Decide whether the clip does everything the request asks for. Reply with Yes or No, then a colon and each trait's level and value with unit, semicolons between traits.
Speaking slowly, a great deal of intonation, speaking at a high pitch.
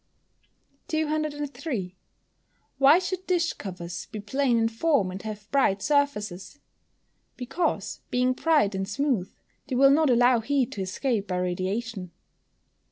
Yes: slow, 125 wpm; wide, 6.5 semitones; high, 245 Hz